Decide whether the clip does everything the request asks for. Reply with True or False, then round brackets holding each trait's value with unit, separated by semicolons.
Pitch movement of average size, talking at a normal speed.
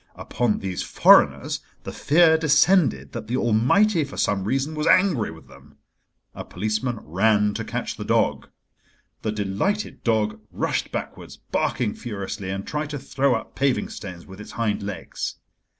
False (6.0 semitones; 155 wpm)